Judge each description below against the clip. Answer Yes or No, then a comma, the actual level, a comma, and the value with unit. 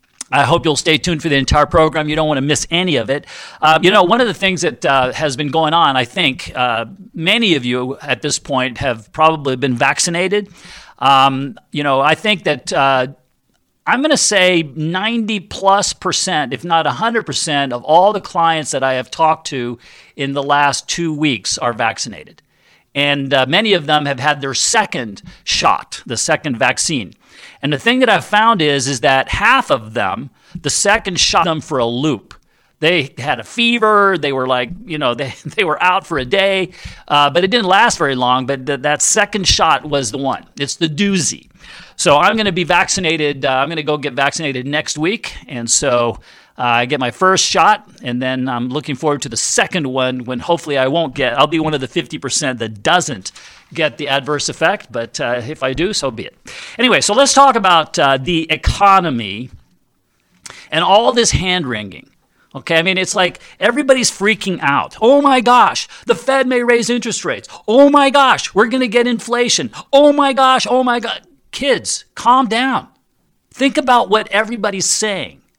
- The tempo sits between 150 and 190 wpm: No, average, 200 wpm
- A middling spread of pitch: No, wide, 6.6 semitones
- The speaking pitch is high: No, medium, 155 Hz